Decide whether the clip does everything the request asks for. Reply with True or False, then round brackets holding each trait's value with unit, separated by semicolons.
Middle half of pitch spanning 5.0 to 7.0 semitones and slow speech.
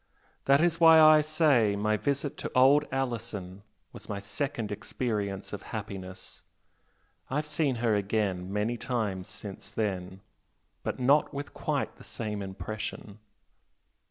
True (5.6 semitones; 130 wpm)